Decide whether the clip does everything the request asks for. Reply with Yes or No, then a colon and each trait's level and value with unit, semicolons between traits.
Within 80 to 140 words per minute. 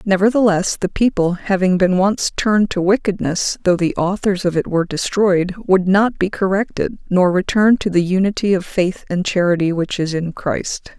No: average, 180 wpm